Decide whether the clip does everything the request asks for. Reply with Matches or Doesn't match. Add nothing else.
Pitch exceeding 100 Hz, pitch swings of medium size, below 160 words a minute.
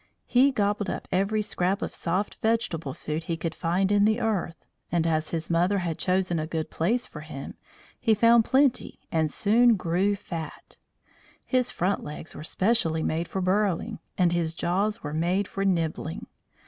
Doesn't match